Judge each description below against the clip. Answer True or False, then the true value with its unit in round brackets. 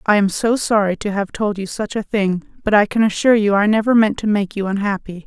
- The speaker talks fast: True (260 wpm)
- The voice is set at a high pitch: True (205 Hz)